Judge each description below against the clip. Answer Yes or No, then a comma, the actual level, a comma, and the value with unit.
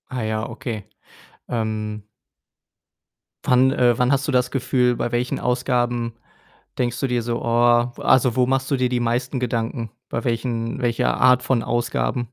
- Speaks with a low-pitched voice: Yes, low, 120 Hz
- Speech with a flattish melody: Yes, narrow, 1.6 semitones